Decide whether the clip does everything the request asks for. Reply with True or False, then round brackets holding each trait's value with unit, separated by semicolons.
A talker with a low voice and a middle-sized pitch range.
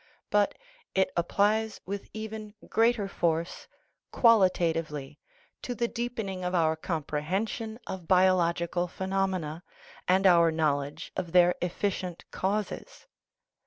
False (185 Hz; 3.6 semitones)